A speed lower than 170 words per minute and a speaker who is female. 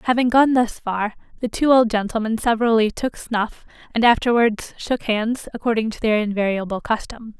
Yes: average, 160 wpm; female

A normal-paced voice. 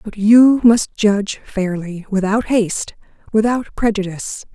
No: slow, 120 wpm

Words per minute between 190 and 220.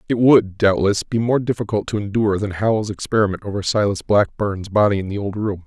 Yes: average, 200 wpm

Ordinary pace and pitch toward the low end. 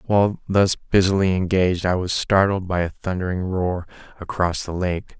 Yes: average, 160 wpm; very low, 90 Hz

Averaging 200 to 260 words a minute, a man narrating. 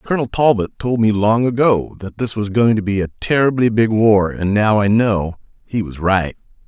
Yes: fast, 205 wpm; male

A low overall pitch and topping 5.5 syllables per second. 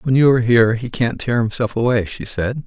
Yes: low, 120 Hz; 5.8 syllables/s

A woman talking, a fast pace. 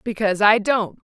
No: female; average, 165 wpm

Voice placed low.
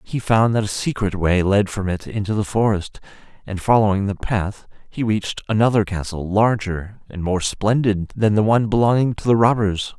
Yes: low, 105 Hz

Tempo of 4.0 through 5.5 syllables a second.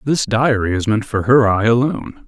Yes: 5.2 syllables/s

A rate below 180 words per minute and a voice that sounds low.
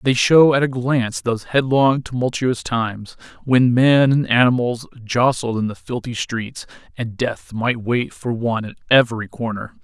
Yes: average, 165 wpm; low, 120 Hz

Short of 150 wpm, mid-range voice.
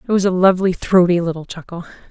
No: average, 200 wpm; medium, 180 Hz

